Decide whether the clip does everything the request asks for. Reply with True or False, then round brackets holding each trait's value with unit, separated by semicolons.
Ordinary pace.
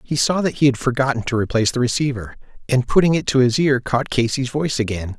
False (230 wpm)